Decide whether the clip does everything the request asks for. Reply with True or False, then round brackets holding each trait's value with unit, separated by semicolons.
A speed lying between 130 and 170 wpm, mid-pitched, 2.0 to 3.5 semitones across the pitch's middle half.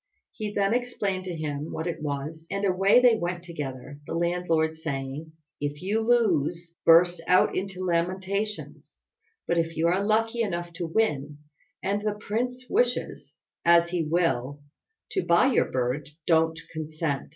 False (150 wpm; 170 Hz; 4.0 semitones)